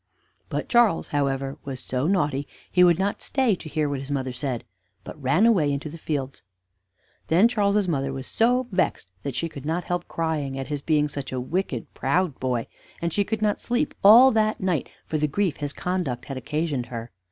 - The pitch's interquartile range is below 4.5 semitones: No, wide, 5.6 semitones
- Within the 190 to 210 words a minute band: Yes, average, 200 wpm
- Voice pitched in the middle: Yes, medium, 150 Hz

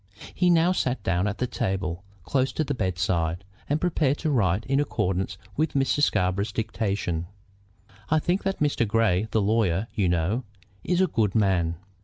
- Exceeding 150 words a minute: Yes, average, 165 wpm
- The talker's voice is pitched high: No, low, 110 Hz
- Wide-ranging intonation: Yes, wide, 7.3 semitones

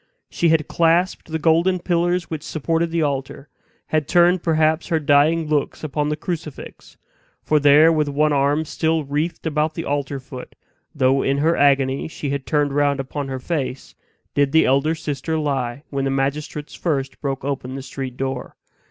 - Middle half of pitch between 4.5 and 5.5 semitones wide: No, average, 2.7 semitones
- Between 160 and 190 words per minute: Yes, average, 175 wpm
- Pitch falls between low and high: Yes, medium, 150 Hz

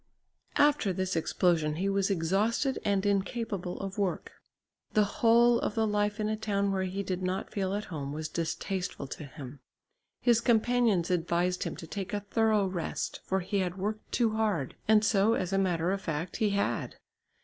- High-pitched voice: Yes, high, 195 Hz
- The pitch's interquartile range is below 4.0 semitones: Yes, average, 3.2 semitones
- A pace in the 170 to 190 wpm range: Yes, average, 180 wpm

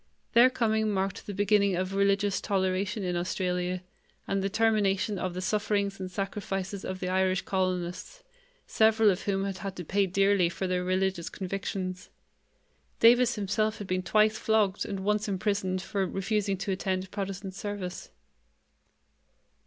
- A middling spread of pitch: No, narrow, 1.8 semitones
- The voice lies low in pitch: No, high, 195 Hz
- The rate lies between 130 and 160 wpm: Yes, average, 150 wpm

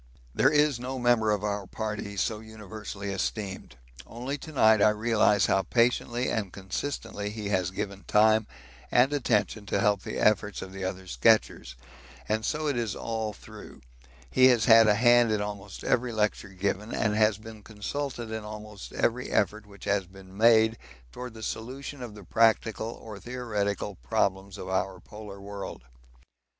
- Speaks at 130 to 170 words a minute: Yes, average, 165 wpm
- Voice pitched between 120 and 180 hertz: No, low, 105 Hz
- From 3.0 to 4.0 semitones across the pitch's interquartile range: No, narrow, 2.4 semitones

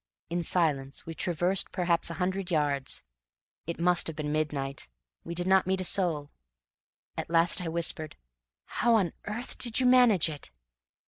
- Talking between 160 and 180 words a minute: Yes, average, 165 wpm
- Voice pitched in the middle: Yes, medium, 170 Hz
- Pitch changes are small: No, average, 3.4 semitones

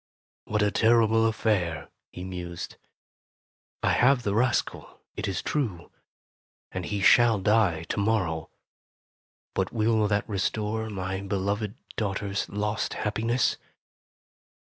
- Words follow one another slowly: Yes, slow, 120 wpm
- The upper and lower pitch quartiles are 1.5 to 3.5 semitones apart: Yes, average, 2.7 semitones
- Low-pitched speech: Yes, low, 105 Hz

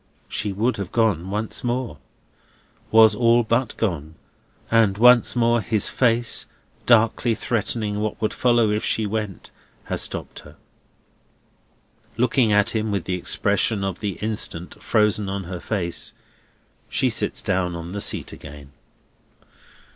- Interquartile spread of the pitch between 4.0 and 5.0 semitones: No, average, 3.1 semitones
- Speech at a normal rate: No, slow, 130 wpm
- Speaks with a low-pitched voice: Yes, low, 105 Hz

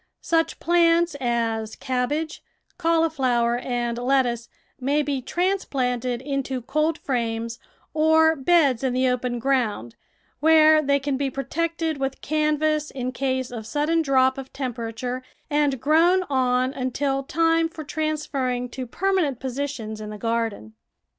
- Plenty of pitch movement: No, average, 3.9 semitones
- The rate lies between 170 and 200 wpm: No, slow, 135 wpm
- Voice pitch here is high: Yes, very high, 270 Hz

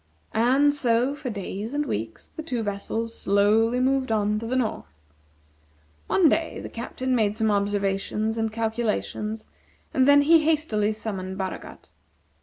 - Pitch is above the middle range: Yes, high, 225 Hz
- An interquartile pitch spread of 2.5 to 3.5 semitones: No, average, 3.9 semitones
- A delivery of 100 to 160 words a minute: Yes, average, 145 wpm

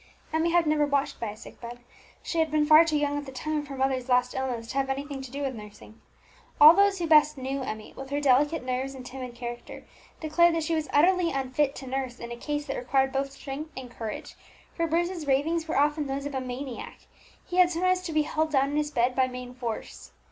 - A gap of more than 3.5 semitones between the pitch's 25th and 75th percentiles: No, average, 3.2 semitones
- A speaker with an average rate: No, fast, 245 wpm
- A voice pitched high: Yes, very high, 275 Hz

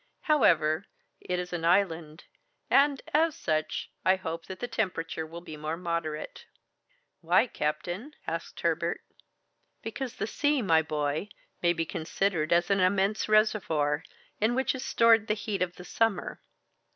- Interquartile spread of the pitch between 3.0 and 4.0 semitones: No, average, 5.2 semitones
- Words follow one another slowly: No, average, 150 wpm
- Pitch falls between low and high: Yes, medium, 180 Hz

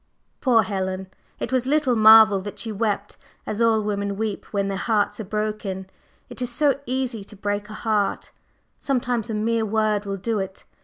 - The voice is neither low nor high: No, high, 215 Hz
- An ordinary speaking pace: Yes, average, 185 wpm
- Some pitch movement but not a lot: No, narrow, 2.3 semitones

